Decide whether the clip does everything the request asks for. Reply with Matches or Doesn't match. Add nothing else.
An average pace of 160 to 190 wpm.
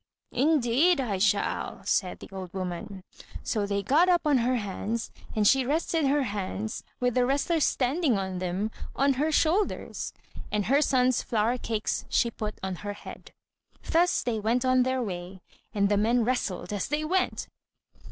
Matches